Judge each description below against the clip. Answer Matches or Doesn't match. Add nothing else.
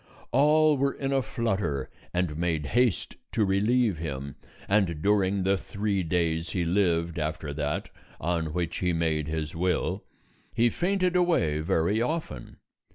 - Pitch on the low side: Matches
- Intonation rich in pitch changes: Matches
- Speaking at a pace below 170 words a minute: Matches